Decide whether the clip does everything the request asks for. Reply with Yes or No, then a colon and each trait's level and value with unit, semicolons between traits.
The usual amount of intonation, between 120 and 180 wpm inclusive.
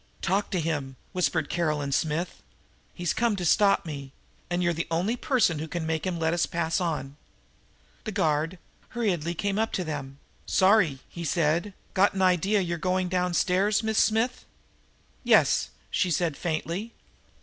Yes: average, 3.4 semitones; average, 160 wpm